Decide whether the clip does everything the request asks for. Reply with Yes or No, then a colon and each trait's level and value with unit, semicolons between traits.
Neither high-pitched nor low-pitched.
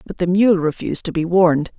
Yes: medium, 175 Hz